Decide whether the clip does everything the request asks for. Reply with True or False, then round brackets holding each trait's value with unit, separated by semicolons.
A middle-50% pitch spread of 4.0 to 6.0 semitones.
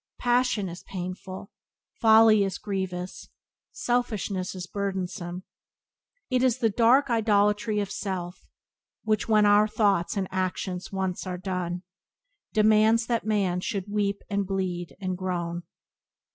False (2.9 semitones)